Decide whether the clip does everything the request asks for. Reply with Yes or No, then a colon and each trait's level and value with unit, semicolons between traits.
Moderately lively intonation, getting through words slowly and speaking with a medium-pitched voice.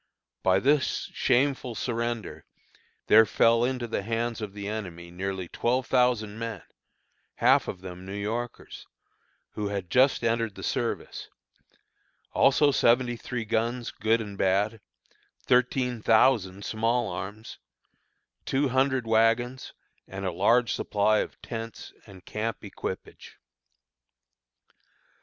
No: average, 3.2 semitones; slow, 120 wpm; low, 115 Hz